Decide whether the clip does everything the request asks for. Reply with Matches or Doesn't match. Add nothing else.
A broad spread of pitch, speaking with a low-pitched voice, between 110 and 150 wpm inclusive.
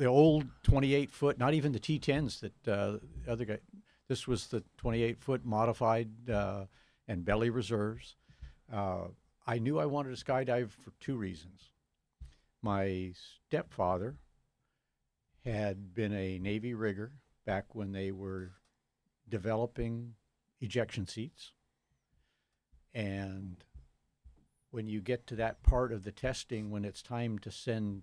Doesn't match